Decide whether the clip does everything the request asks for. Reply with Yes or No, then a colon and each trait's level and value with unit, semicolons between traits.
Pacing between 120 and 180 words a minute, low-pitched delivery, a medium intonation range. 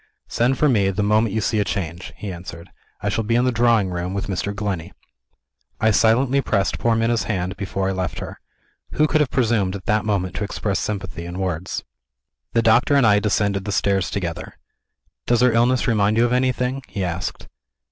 No: average, 200 wpm; low, 105 Hz; average, 3.6 semitones